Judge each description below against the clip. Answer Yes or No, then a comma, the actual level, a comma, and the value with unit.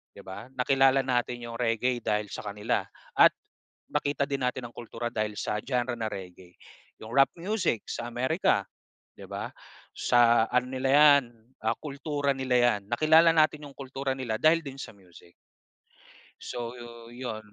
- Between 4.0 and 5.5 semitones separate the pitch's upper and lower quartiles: No, average, 3.2 semitones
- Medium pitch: No, low, 125 Hz